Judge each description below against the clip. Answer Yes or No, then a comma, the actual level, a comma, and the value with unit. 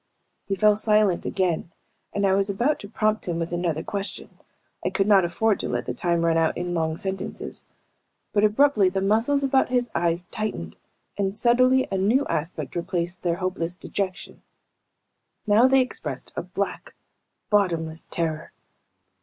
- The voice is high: Yes, high, 195 Hz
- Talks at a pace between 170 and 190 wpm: No, average, 160 wpm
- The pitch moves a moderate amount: Yes, average, 3.9 semitones